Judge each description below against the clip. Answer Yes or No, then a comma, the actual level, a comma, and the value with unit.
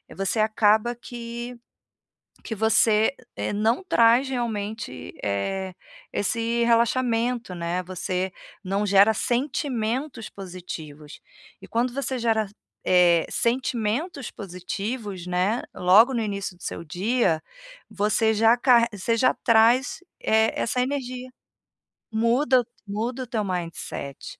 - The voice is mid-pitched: No, high, 220 Hz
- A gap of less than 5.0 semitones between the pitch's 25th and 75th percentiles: Yes, average, 3.9 semitones